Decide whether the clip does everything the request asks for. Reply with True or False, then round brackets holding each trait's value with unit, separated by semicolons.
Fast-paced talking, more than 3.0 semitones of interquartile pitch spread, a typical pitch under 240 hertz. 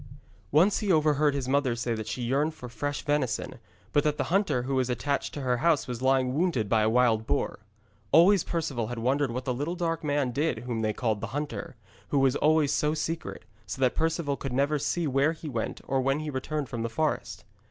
True (220 wpm; 3.6 semitones; 140 Hz)